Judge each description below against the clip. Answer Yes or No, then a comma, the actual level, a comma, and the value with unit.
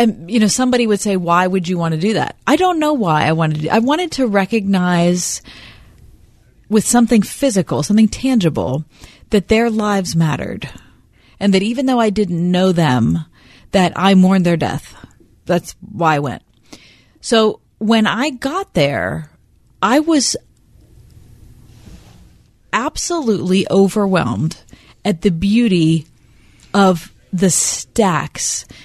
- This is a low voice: No, medium, 185 Hz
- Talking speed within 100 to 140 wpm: Yes, slow, 135 wpm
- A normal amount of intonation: No, wide, 6.6 semitones